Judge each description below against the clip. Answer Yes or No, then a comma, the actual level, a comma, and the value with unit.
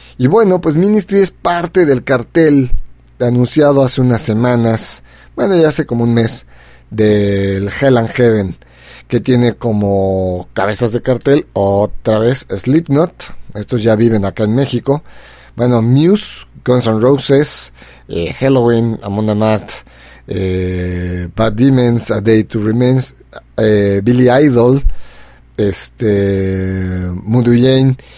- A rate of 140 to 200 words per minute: No, slow, 125 wpm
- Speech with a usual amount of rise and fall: Yes, average, 4.9 semitones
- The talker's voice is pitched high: No, low, 115 Hz